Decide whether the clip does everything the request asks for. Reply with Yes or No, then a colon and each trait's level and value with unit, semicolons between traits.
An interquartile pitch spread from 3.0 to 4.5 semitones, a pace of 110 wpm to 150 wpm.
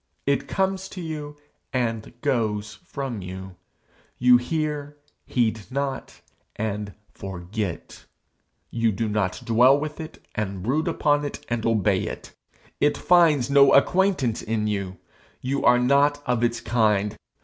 No: wide, 5.4 semitones; slow, 135 wpm